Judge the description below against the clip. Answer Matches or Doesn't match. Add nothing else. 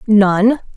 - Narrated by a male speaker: Doesn't match